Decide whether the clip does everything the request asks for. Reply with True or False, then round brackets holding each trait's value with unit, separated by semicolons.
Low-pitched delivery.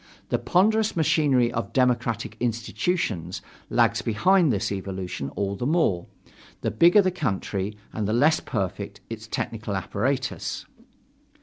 True (115 Hz)